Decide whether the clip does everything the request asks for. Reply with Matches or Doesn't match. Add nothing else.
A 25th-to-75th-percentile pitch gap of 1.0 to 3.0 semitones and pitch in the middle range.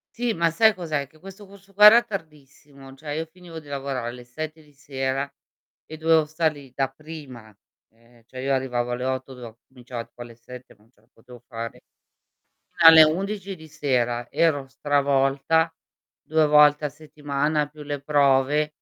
Doesn't match